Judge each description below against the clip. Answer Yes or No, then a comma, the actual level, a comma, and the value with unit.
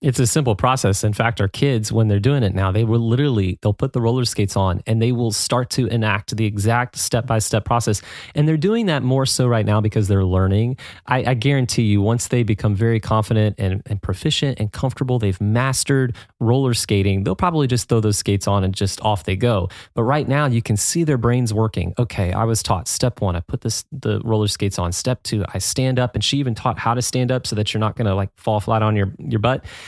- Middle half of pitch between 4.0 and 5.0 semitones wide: No, average, 3.5 semitones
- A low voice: Yes, low, 115 Hz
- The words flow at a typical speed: No, fast, 265 wpm